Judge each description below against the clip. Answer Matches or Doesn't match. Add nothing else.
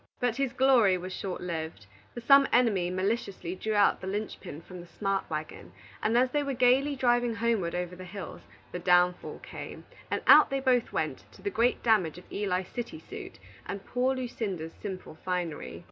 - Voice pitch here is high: Matches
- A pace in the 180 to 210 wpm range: Matches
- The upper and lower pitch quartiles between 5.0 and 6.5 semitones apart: Matches